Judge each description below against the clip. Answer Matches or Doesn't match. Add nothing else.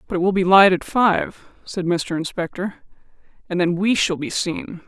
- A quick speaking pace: Doesn't match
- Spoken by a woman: Matches